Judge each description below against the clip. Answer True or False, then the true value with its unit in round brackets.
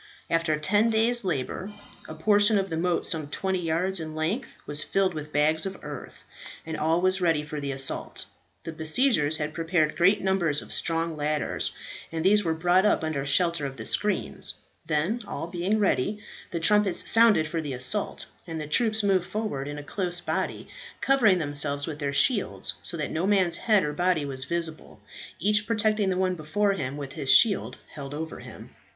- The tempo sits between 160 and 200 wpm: True (190 wpm)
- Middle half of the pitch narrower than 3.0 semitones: False (4.4 semitones)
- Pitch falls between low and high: True (165 Hz)